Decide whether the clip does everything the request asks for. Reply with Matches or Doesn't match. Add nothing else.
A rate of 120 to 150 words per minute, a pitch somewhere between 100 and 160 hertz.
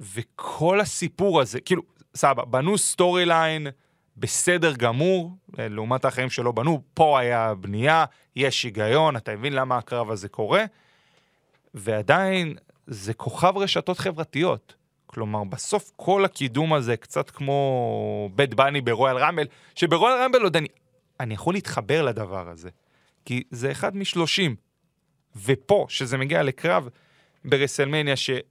Matches